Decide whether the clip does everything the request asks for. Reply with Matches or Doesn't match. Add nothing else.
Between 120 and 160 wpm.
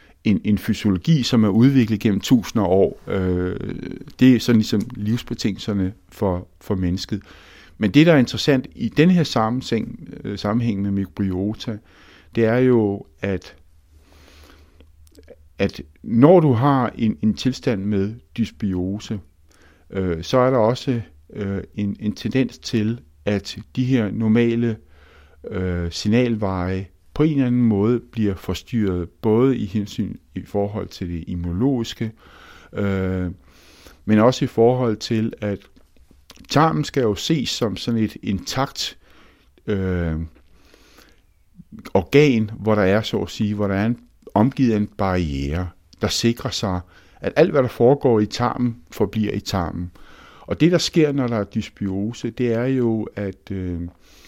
Matches